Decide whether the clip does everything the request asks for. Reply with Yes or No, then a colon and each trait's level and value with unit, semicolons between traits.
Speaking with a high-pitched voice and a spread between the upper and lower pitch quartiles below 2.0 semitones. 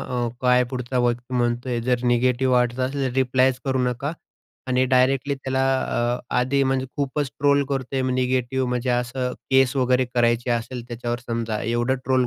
No: low, 125 Hz; narrow, 1.5 semitones